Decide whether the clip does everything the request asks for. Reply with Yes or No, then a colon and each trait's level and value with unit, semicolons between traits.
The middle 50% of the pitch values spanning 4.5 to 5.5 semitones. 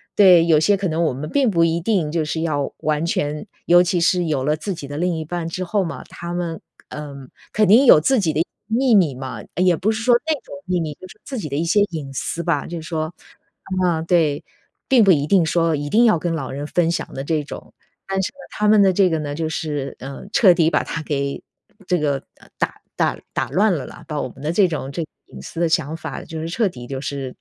No: average, 3.5 semitones